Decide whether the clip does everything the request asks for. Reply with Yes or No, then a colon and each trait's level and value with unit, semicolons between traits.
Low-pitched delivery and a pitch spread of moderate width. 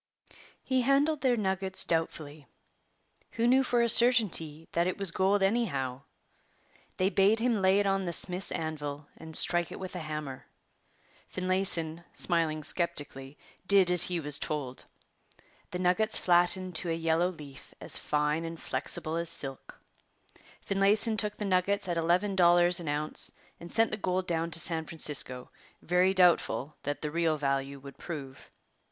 No: medium, 175 Hz; average, 4.0 semitones